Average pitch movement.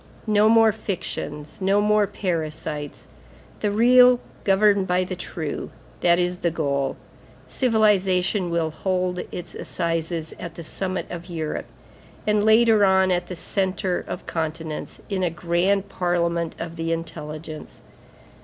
Yes: average, 3.3 semitones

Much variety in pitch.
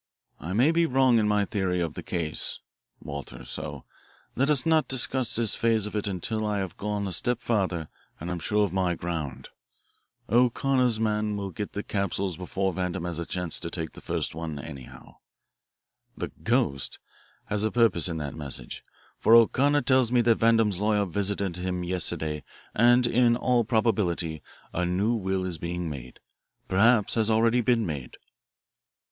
No: average, 5.0 semitones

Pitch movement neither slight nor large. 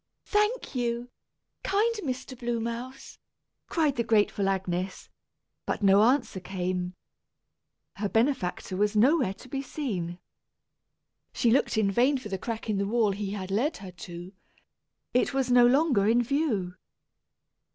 Yes: average, 4.9 semitones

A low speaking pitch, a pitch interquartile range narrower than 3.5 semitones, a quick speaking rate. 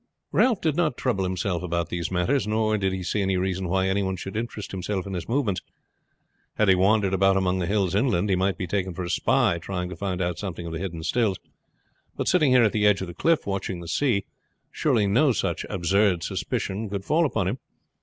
Yes: very low, 95 Hz; average, 3.0 semitones; fast, 225 wpm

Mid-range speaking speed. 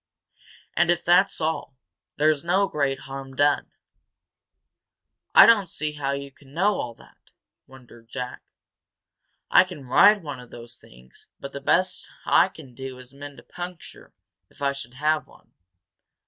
Yes: average, 150 wpm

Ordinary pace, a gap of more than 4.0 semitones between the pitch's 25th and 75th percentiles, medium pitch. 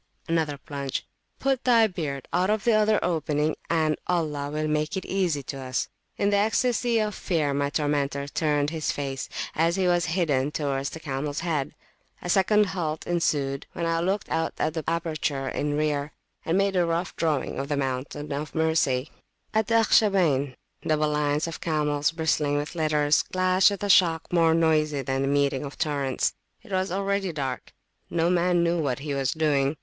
No: average, 180 wpm; average, 3.6 semitones; medium, 155 Hz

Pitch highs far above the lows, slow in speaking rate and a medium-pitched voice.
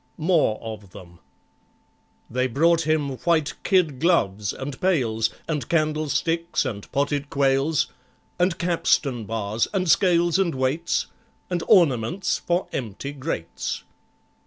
Yes: wide, 6.2 semitones; slow, 115 wpm; medium, 145 Hz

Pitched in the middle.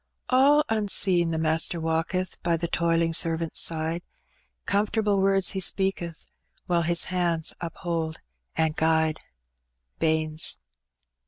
Yes: medium, 170 Hz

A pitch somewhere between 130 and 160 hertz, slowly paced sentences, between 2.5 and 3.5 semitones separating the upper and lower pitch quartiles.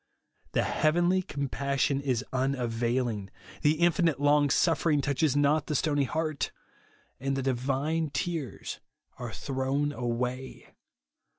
Yes: medium, 140 Hz; slow, 110 wpm; average, 2.9 semitones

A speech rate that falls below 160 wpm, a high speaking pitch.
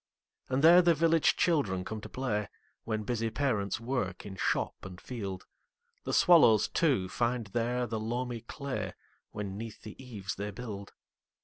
No: average, 140 wpm; low, 115 Hz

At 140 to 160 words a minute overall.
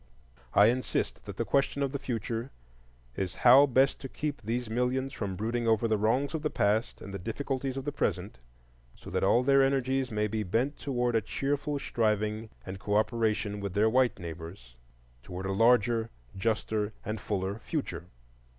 No: average, 175 wpm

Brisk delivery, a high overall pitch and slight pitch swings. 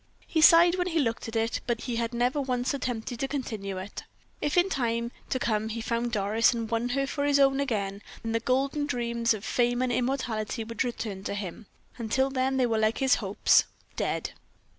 No: fast, 210 wpm; high, 240 Hz; average, 3.1 semitones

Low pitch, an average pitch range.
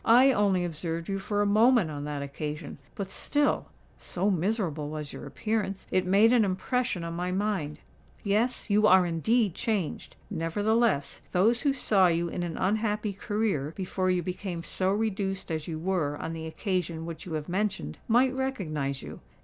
No: high, 190 Hz; average, 4.5 semitones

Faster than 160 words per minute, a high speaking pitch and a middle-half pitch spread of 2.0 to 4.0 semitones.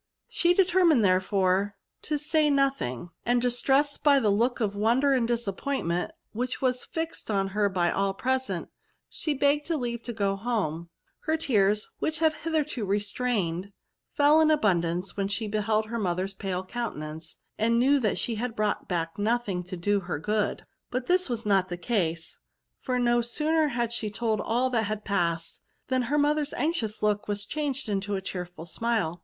No: average, 175 wpm; high, 220 Hz; wide, 5.4 semitones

